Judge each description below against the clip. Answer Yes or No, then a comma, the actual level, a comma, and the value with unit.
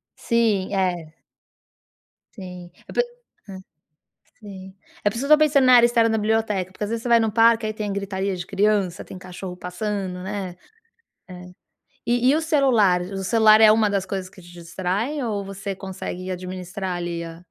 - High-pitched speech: Yes, high, 200 Hz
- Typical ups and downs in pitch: Yes, average, 3.4 semitones